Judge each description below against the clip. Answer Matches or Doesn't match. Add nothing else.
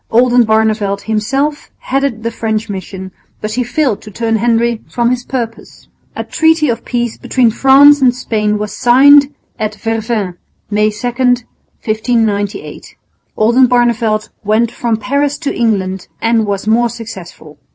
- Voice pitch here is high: Matches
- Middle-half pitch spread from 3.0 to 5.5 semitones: Doesn't match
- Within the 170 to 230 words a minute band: Doesn't match